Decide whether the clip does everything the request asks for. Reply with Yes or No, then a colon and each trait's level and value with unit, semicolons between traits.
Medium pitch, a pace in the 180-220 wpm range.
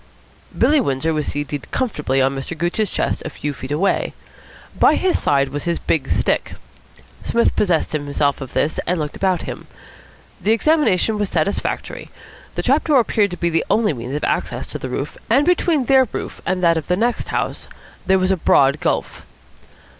Yes: medium, 175 Hz; average, 185 wpm